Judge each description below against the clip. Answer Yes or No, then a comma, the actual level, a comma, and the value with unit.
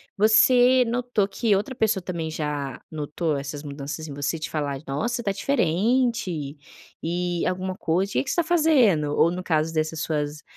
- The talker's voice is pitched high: No, medium, 175 Hz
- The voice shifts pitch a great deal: Yes, wide, 7.0 semitones